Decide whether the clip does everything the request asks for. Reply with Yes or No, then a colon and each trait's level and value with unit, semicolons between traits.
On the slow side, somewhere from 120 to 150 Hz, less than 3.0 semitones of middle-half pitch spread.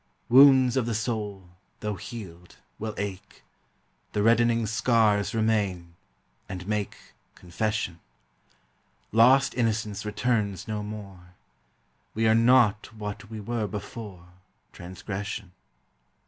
No: slow, 105 wpm; low, 105 Hz; narrow, 2.5 semitones